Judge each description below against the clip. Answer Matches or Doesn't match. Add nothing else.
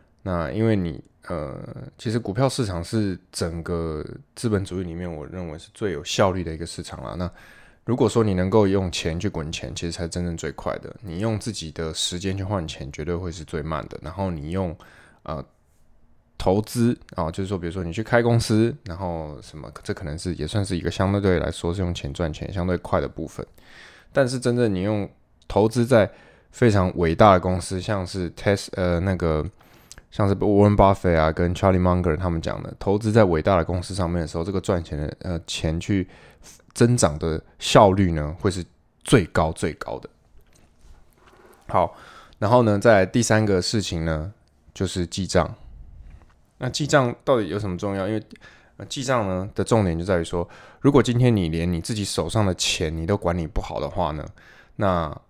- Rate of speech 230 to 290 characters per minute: Matches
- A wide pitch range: Doesn't match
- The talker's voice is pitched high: Doesn't match